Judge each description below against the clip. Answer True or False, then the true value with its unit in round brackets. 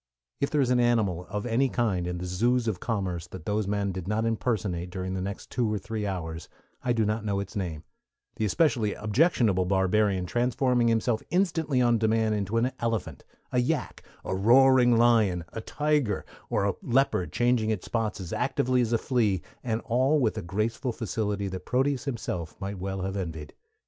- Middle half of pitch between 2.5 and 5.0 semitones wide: True (4.2 semitones)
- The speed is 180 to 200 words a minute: True (190 wpm)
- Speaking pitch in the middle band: False (110 Hz)